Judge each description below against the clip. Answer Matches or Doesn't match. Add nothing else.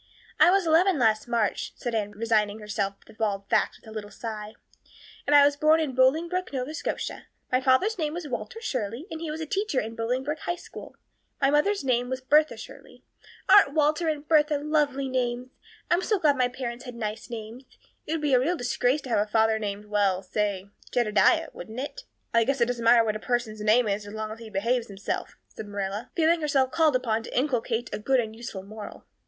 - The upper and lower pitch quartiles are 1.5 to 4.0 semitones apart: Doesn't match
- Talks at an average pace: Doesn't match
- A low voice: Doesn't match